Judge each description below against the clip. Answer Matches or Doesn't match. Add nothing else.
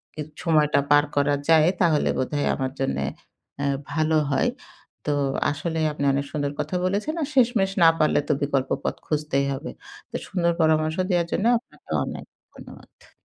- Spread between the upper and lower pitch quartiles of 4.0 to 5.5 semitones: Doesn't match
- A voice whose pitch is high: Doesn't match